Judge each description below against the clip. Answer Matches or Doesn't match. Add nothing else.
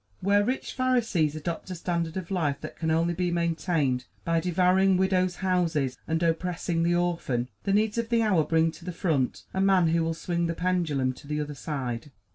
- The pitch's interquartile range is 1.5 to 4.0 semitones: Matches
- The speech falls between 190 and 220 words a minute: Matches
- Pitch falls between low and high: Matches